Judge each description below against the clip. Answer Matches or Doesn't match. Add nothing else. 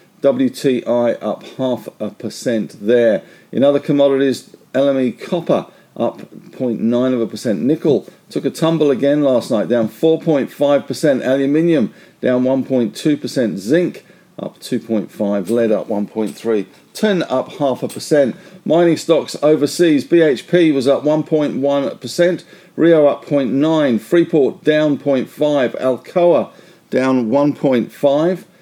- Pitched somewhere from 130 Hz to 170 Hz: Matches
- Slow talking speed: Matches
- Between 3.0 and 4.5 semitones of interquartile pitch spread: Matches